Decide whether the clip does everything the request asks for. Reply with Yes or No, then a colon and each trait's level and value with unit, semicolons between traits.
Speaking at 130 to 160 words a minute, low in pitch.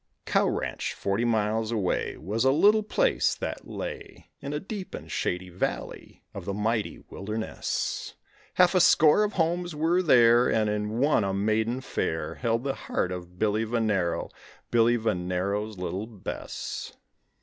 Yes: average, 150 wpm; low, 110 Hz